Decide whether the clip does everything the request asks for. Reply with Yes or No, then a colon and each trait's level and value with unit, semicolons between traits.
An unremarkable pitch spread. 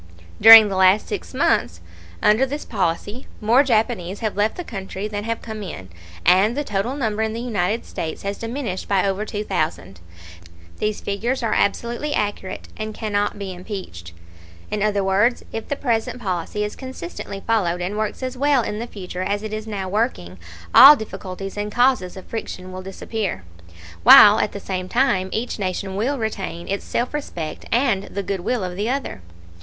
Yes: average, 3.4 semitones